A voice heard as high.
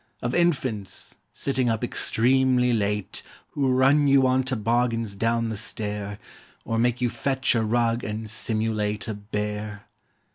No: low, 115 Hz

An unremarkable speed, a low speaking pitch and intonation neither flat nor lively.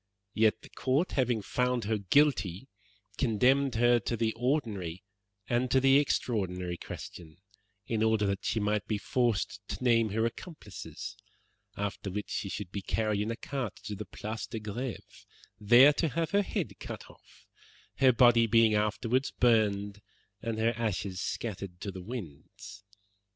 Yes: average, 155 wpm; low, 110 Hz; average, 3.4 semitones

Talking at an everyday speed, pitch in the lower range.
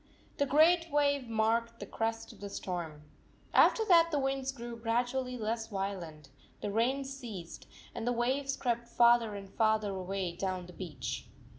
No: average, 160 wpm; high, 230 Hz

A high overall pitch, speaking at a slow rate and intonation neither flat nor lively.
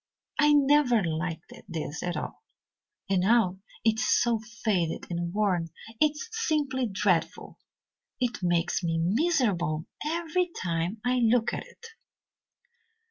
No: high, 215 Hz; slow, 130 wpm; wide, 7.2 semitones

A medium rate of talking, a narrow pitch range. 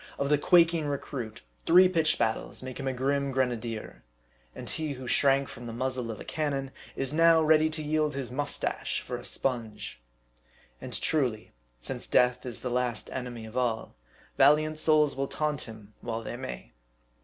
No: average, 170 wpm; average, 4.0 semitones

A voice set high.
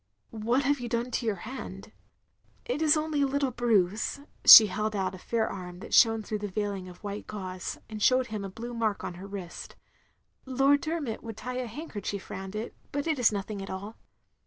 Yes: high, 220 Hz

